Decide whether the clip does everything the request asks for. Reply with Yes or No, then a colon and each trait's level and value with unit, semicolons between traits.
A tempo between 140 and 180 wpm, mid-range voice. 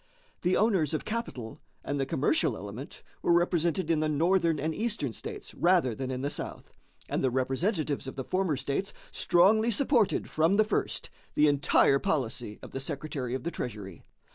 Yes: average, 175 wpm; medium, 155 Hz